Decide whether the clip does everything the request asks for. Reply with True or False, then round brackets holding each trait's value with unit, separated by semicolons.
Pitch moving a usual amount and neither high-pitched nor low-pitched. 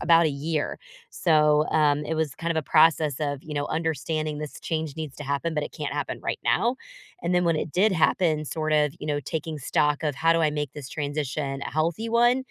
False (1.8 semitones; 155 Hz)